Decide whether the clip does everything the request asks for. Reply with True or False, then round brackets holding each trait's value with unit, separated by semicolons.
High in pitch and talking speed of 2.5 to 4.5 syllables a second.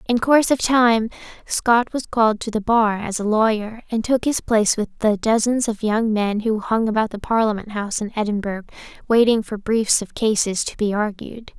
False (220 Hz; 5.1 syllables/s)